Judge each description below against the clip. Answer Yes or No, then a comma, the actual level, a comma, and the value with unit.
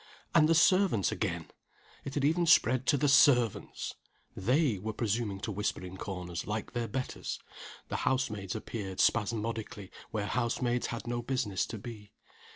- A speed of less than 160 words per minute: No, average, 165 wpm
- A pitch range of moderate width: Yes, average, 4.2 semitones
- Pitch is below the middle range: Yes, low, 115 Hz